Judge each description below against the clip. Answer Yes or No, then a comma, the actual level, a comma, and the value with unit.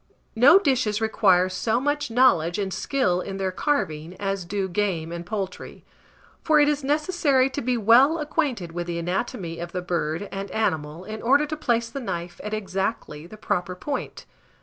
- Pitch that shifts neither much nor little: No, wide, 6.8 semitones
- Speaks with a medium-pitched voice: No, high, 205 Hz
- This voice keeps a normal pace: Yes, average, 175 wpm